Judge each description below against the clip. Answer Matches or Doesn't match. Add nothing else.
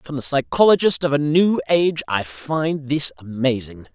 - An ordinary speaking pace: Matches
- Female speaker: Doesn't match